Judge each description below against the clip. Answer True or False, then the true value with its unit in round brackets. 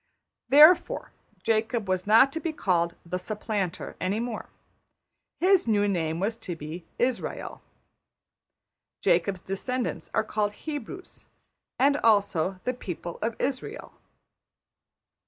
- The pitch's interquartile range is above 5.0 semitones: True (5.6 semitones)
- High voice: True (215 Hz)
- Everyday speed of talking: False (115 wpm)